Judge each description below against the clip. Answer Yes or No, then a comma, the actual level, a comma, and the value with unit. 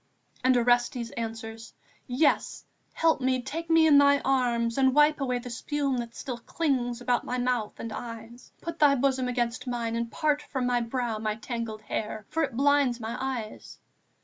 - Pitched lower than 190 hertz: No, high, 245 Hz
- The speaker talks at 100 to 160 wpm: No, average, 175 wpm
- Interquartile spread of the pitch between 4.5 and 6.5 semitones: No, average, 3.0 semitones